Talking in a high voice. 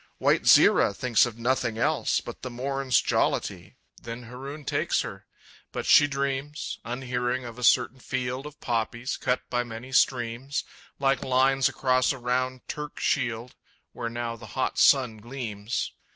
No: low, 125 Hz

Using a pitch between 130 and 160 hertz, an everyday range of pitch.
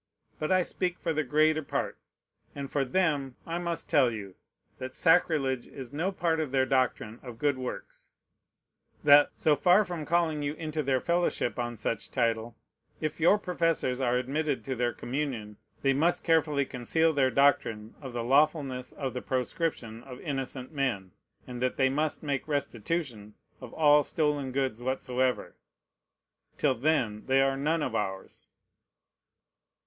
Yes: medium, 140 Hz; average, 3.7 semitones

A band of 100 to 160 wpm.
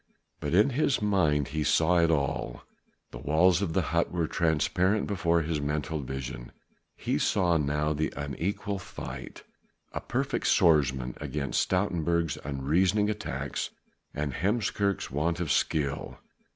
Yes: slow, 135 wpm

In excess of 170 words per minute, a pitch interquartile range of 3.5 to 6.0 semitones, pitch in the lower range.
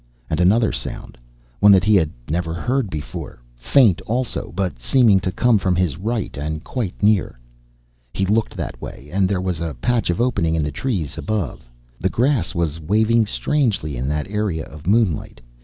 Yes: average, 180 wpm; wide, 5.5 semitones; very low, 95 Hz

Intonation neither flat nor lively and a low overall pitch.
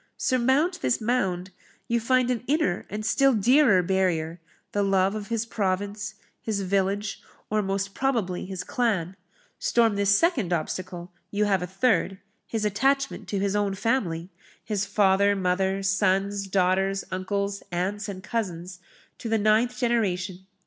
No: average, 3.2 semitones; high, 200 Hz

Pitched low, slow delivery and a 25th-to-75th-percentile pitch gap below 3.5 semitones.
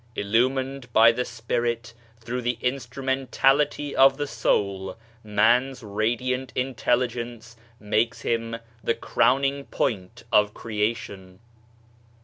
Yes: low, 120 Hz; slow, 100 wpm; average, 2.9 semitones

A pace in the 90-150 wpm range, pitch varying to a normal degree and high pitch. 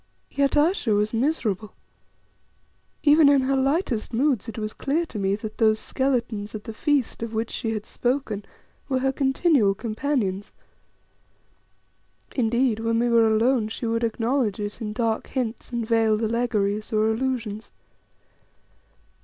Yes: average, 145 wpm; average, 3.6 semitones; high, 230 Hz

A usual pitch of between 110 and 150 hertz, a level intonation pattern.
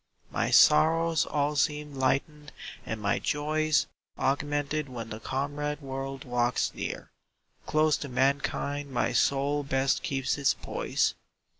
Yes: medium, 140 Hz; narrow, 1.9 semitones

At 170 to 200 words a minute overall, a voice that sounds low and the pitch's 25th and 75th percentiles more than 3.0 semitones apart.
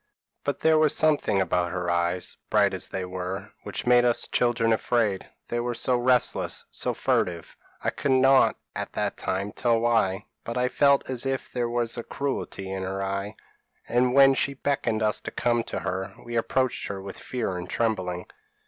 Yes: average, 185 wpm; low, 115 Hz; average, 4.8 semitones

